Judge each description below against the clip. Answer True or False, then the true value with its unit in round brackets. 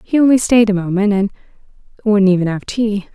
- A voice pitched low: False (205 Hz)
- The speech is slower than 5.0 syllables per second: False (5.7 syllables/s)